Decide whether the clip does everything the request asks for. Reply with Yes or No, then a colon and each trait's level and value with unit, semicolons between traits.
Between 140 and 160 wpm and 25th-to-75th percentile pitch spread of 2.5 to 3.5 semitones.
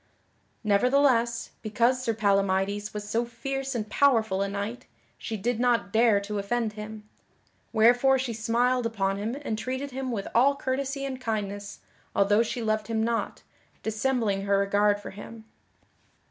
Yes: average, 150 wpm; average, 3.2 semitones